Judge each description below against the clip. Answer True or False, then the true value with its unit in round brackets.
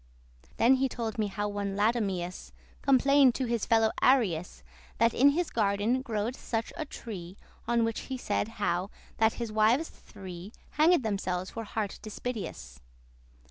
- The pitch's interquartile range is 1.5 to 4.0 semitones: True (3.7 semitones)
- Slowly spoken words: False (155 wpm)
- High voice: True (220 Hz)